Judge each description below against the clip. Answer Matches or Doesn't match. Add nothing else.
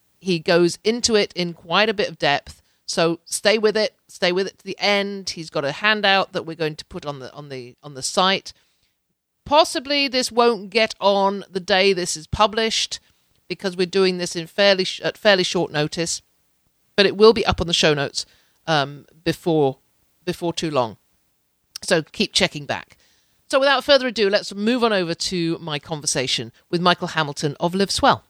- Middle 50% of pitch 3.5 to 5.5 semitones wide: Matches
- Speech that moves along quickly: Doesn't match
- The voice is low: Doesn't match